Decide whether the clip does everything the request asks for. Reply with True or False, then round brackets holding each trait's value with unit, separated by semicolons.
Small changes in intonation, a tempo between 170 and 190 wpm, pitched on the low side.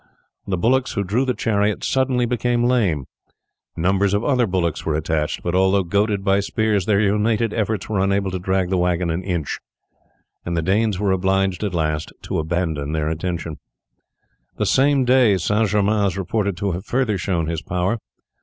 False (3.7 semitones; 180 wpm; 95 Hz)